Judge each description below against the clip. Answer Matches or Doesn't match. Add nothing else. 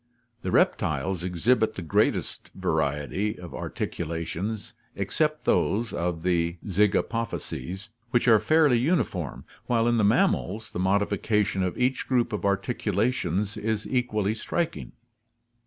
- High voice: Doesn't match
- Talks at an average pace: Doesn't match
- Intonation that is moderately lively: Matches